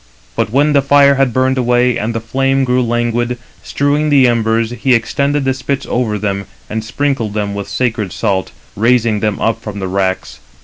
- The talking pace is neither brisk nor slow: Yes, average, 185 wpm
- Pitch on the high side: No, low, 120 Hz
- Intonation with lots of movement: No, average, 3.7 semitones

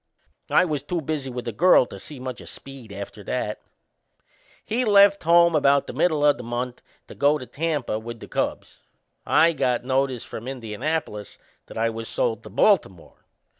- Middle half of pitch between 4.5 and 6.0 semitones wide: Yes, average, 5.2 semitones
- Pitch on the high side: No, low, 135 Hz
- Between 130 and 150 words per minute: No, average, 180 wpm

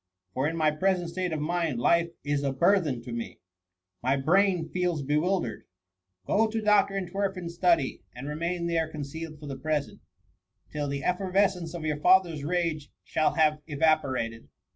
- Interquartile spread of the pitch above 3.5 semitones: Yes, average, 4.0 semitones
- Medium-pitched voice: Yes, medium, 160 Hz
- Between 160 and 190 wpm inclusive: Yes, average, 175 wpm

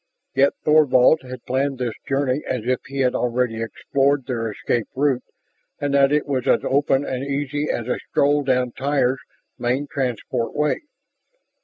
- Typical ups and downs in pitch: No, narrow, 2.2 semitones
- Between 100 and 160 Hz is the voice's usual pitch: Yes, low, 135 Hz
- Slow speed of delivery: No, average, 160 wpm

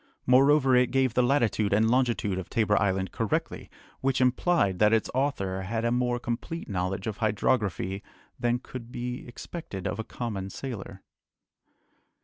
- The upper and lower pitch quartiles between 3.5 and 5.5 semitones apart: Yes, average, 4.2 semitones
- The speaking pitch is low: Yes, low, 115 Hz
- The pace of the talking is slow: No, average, 150 wpm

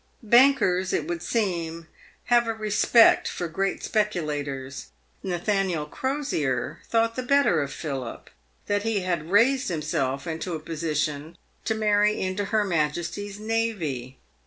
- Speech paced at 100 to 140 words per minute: Yes, slow, 135 wpm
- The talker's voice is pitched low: No, medium, 185 Hz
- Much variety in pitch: Yes, wide, 5.9 semitones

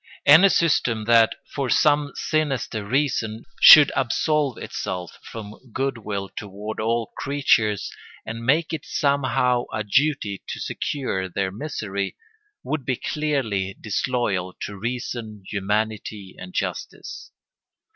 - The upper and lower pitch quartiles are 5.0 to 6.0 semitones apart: Yes, average, 5.3 semitones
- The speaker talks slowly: Yes, slow, 115 wpm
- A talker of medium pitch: No, low, 115 Hz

